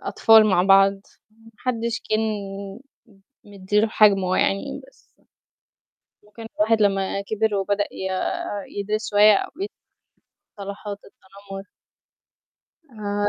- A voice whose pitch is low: No, high, 205 Hz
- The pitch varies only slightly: Yes, narrow, 1.8 semitones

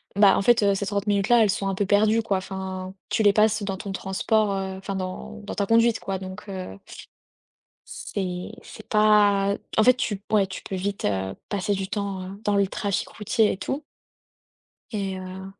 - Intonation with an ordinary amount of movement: No, narrow, 1.9 semitones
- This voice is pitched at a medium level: No, high, 200 Hz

